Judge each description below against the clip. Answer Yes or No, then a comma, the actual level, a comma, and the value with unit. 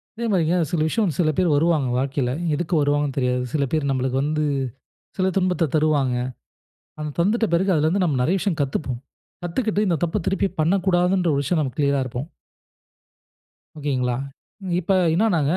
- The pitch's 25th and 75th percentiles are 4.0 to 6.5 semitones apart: Yes, average, 4.5 semitones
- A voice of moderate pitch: Yes, medium, 155 Hz